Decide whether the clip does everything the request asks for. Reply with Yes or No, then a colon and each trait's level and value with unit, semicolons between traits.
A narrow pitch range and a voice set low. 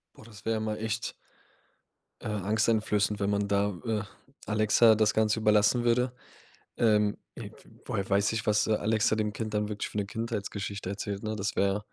Yes: narrow, 1.3 semitones; low, 105 Hz